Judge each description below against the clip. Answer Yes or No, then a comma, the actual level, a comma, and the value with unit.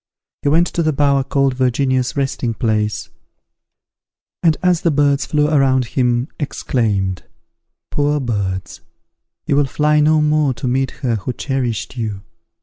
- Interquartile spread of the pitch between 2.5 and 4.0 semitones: Yes, average, 3.7 semitones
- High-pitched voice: No, low, 135 Hz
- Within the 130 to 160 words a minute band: Yes, average, 145 wpm